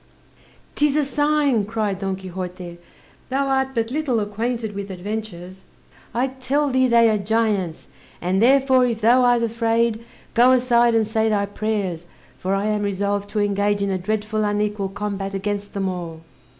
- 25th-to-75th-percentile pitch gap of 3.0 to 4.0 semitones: Yes, average, 3.3 semitones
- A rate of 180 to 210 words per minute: No, average, 165 wpm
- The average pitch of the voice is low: No, high, 215 Hz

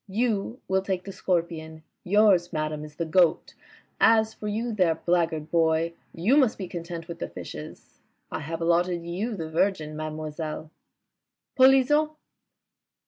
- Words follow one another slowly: No, average, 145 wpm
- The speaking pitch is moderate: Yes, medium, 170 Hz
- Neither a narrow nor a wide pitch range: Yes, average, 4.3 semitones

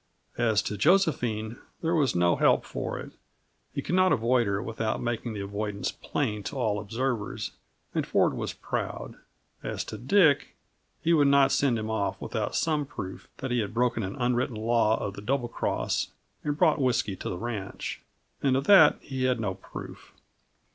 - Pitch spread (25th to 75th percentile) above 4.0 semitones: Yes, average, 4.4 semitones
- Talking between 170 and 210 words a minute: Yes, average, 180 wpm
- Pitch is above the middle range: No, low, 120 Hz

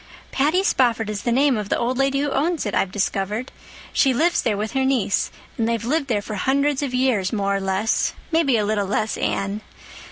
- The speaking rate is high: Yes, fast, 210 wpm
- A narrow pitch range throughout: No, average, 4.8 semitones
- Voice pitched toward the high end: Yes, high, 235 Hz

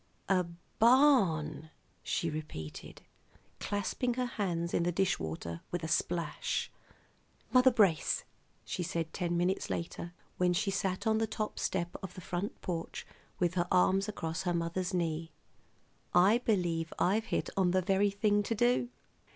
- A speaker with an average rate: Yes, average, 150 wpm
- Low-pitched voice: No, medium, 180 Hz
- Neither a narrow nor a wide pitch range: Yes, average, 3.3 semitones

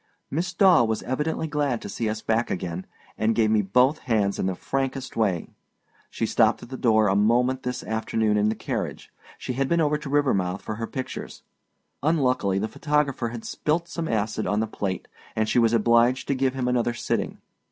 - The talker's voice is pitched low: Yes, low, 120 Hz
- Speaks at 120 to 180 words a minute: No, average, 200 wpm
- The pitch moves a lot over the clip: No, average, 3.9 semitones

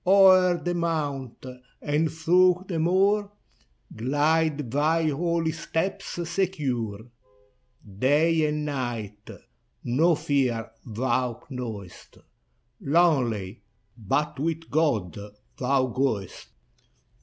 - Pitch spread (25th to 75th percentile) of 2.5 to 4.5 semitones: No, average, 5.3 semitones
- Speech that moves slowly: Yes, slow, 90 wpm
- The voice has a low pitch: No, medium, 150 Hz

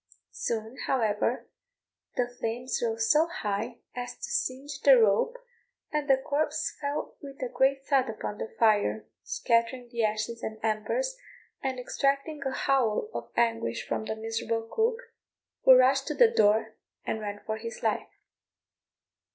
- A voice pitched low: No, high, 245 Hz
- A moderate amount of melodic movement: Yes, average, 3.8 semitones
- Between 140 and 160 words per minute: Yes, average, 150 wpm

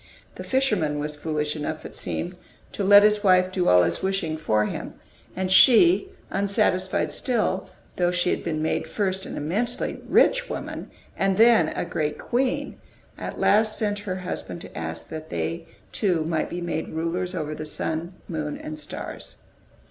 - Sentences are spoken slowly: No, average, 170 wpm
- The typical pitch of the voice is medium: Yes, medium, 180 Hz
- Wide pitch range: No, average, 4.6 semitones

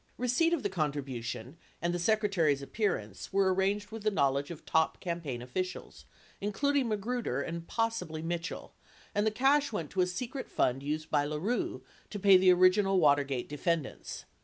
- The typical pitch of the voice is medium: Yes, medium, 180 Hz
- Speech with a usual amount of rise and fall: No, wide, 6.0 semitones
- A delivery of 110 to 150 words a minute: No, average, 165 wpm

